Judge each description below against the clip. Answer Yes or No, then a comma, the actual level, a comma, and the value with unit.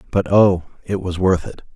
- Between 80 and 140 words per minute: No, fast, 205 wpm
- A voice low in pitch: Yes, very low, 95 Hz